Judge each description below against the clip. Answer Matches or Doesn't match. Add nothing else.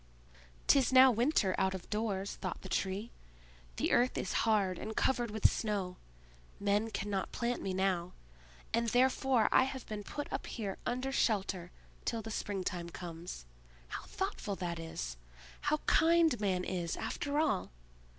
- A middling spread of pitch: Matches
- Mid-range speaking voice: Doesn't match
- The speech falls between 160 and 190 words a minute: Doesn't match